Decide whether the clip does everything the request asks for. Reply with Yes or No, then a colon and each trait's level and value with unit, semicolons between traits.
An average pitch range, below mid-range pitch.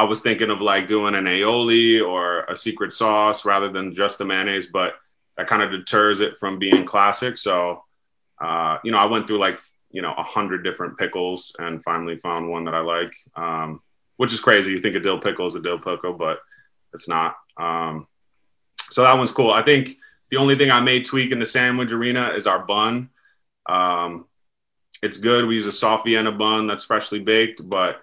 Yes: average, 4.2 semitones; low, 105 Hz